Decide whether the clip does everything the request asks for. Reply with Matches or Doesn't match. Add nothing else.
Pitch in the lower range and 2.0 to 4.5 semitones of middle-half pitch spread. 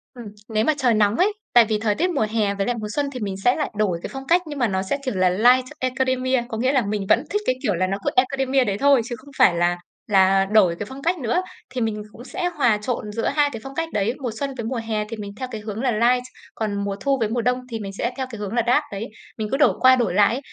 Doesn't match